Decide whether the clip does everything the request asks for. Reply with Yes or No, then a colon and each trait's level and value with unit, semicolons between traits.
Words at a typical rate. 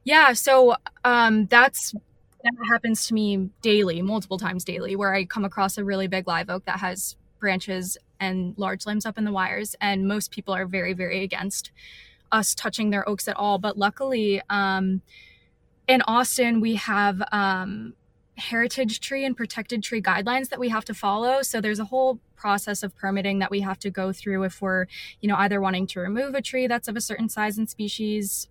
Yes: average, 195 wpm